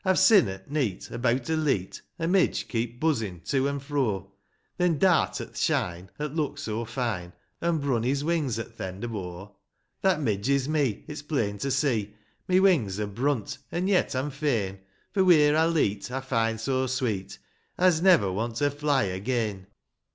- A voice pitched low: Yes, low, 130 Hz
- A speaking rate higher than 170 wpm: Yes, average, 190 wpm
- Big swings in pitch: Yes, wide, 6.3 semitones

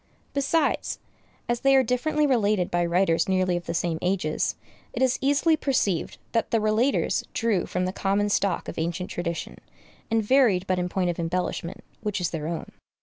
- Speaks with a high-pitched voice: Yes, high, 195 Hz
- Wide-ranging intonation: Yes, wide, 5.7 semitones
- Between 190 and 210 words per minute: No, average, 180 wpm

